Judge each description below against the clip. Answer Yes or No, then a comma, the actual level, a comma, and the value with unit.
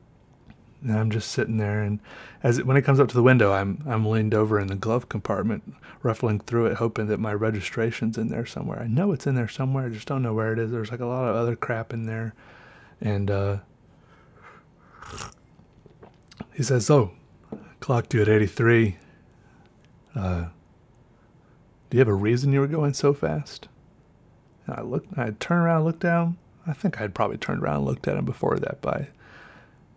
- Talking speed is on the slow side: No, average, 195 wpm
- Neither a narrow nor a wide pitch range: Yes, average, 3.5 semitones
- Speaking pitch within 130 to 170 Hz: No, low, 115 Hz